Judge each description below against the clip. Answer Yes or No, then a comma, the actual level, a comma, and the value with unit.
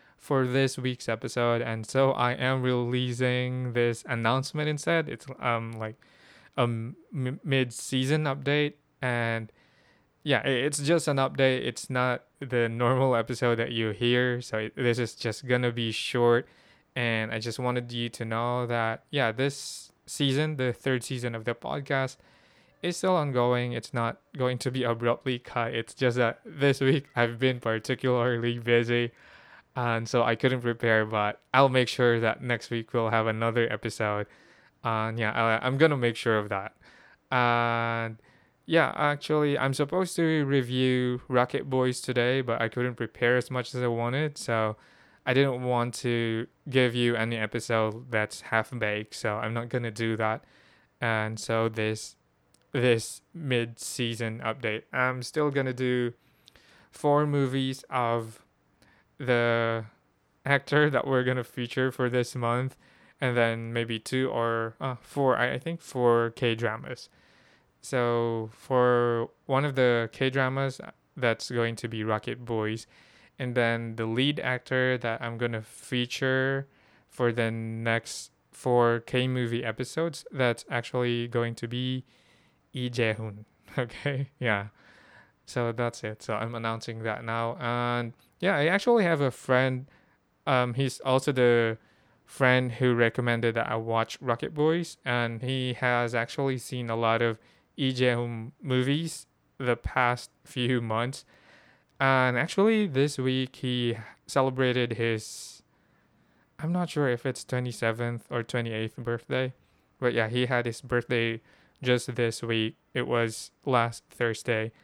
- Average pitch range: No, narrow, 2.2 semitones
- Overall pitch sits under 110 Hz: No, low, 120 Hz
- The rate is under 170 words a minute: Yes, average, 150 wpm